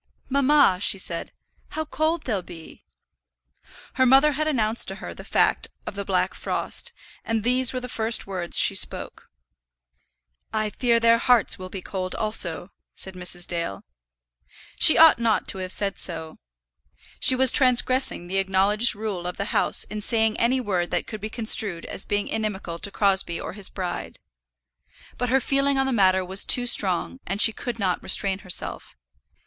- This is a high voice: Yes, high, 215 Hz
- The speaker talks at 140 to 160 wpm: No, average, 175 wpm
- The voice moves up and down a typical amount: Yes, average, 4.9 semitones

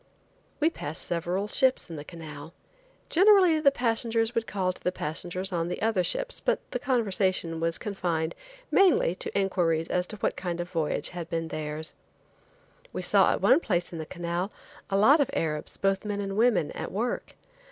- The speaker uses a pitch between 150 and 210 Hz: Yes, medium, 185 Hz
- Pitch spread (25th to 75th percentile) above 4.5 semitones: Yes, average, 5.3 semitones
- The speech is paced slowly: No, average, 185 wpm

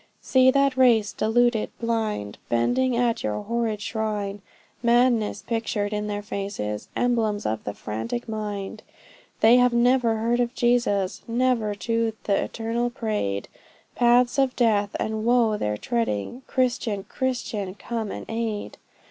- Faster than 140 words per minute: No, slow, 135 wpm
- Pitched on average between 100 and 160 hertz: No, high, 225 Hz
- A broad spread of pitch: No, average, 2.8 semitones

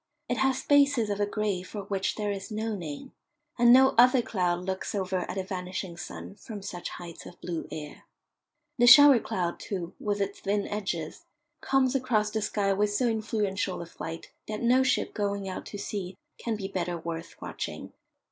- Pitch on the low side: No, high, 205 Hz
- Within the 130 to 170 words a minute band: No, average, 185 wpm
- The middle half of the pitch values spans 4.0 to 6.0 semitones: No, average, 3.6 semitones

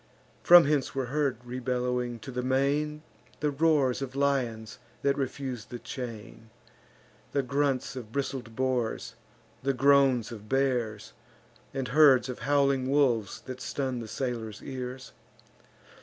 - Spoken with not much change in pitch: Yes, narrow, 2.2 semitones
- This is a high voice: No, low, 130 Hz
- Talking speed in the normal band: No, slow, 130 wpm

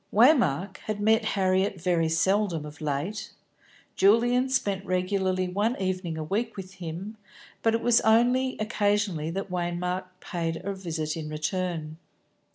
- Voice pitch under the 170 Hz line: No, high, 190 Hz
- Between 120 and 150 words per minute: Yes, average, 140 wpm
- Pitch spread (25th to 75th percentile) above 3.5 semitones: Yes, average, 4.0 semitones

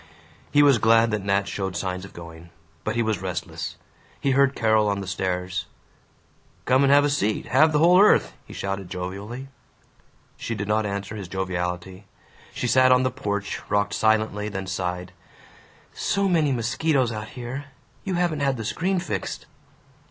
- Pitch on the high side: No, low, 110 Hz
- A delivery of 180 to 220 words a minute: No, average, 165 wpm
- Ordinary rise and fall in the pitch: No, wide, 5.7 semitones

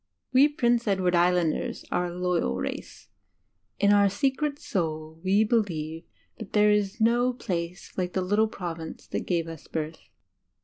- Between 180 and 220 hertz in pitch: Yes, medium, 185 Hz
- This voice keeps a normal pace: Yes, average, 160 wpm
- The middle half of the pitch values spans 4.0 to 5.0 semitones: Yes, average, 4.4 semitones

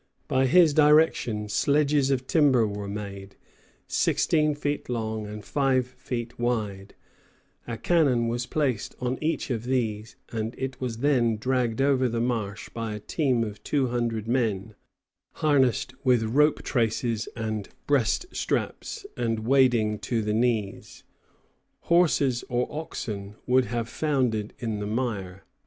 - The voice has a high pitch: No, low, 120 Hz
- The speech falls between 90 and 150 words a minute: Yes, average, 140 wpm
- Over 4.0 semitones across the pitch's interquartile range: No, average, 3.6 semitones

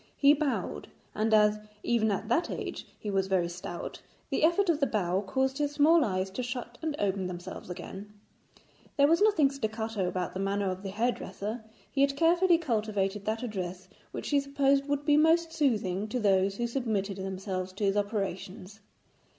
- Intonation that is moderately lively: No, wide, 6.4 semitones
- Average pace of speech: Yes, average, 180 wpm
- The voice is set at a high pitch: Yes, high, 215 Hz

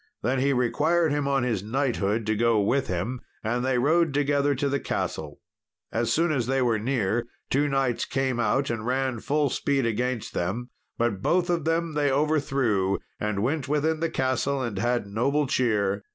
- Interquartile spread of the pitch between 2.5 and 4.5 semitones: Yes, average, 3.9 semitones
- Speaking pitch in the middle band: No, low, 130 Hz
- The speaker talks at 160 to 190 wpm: Yes, average, 180 wpm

